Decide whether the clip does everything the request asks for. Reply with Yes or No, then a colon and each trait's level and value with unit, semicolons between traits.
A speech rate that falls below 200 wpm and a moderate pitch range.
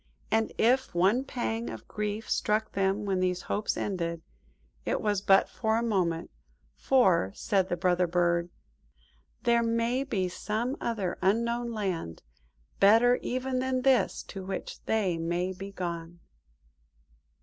Yes: average, 140 wpm; average, 4.4 semitones